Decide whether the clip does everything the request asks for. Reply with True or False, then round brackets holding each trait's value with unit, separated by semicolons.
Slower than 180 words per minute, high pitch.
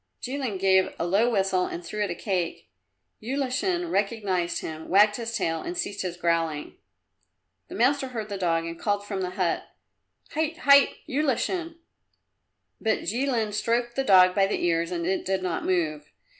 True (170 wpm; 200 Hz)